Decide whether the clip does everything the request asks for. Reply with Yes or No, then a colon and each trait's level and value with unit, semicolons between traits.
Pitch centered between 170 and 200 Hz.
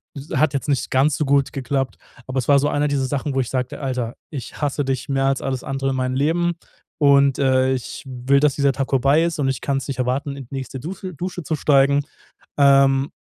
No: low, 135 Hz